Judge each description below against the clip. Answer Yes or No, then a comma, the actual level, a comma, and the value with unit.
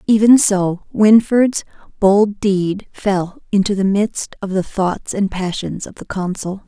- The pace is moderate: Yes, average, 155 wpm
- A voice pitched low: No, high, 200 Hz